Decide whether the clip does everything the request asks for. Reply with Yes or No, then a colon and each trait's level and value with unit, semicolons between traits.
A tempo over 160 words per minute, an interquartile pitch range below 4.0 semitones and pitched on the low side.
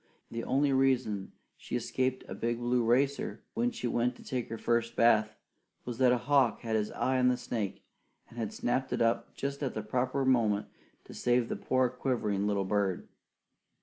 Yes: average, 185 wpm; narrow, 2.5 semitones; low, 120 Hz